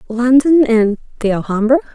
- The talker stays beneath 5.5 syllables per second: Yes, 5.0 syllables/s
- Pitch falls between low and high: No, high, 240 Hz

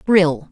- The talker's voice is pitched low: No, medium, 170 Hz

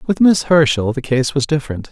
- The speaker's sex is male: Yes, male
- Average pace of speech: No, fast, 220 wpm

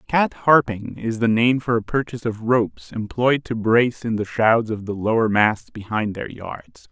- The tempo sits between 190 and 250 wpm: Yes, average, 200 wpm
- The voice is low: Yes, low, 115 Hz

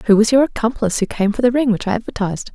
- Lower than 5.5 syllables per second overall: No, 7.5 syllables/s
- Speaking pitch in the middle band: No, high, 220 Hz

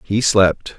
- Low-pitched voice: Yes, low, 100 Hz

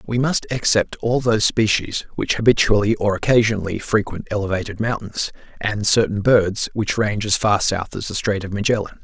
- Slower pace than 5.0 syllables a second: No, 5.4 syllables/s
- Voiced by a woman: No, male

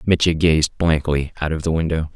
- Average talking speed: Yes, average, 195 wpm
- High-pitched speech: No, very low, 80 Hz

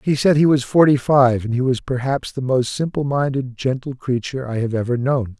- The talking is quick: Yes, fast, 225 wpm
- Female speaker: No, male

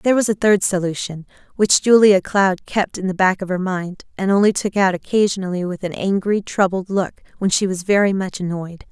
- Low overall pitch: No, high, 190 Hz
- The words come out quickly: Yes, fast, 210 wpm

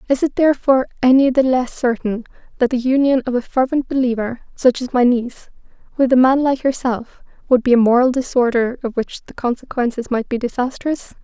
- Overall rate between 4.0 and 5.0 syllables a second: No, 5.6 syllables/s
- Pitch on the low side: No, very high, 250 Hz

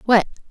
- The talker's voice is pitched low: No, high, 220 Hz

